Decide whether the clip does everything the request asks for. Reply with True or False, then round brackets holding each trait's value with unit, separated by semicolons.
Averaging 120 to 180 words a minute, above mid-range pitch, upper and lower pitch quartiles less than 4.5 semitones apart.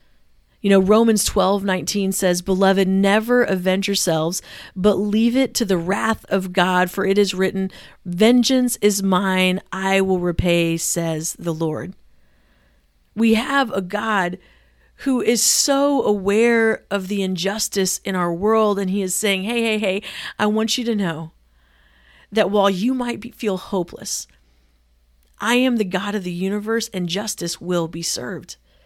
True (160 wpm; 195 Hz; 3.5 semitones)